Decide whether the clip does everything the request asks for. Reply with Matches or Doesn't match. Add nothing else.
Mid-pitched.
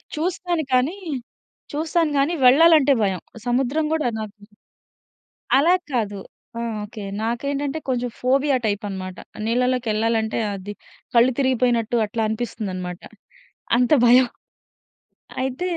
Doesn't match